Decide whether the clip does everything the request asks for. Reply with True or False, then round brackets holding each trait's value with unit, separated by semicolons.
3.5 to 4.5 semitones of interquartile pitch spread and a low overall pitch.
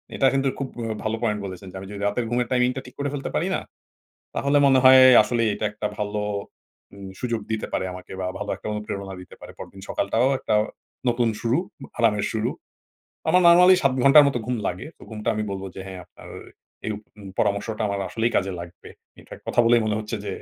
True (3.8 semitones; 110 Hz)